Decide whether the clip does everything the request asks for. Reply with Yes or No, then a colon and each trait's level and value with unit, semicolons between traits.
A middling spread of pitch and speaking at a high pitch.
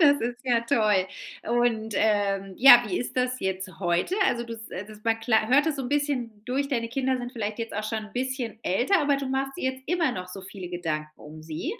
Yes: average, 4.3 semitones; high, 230 Hz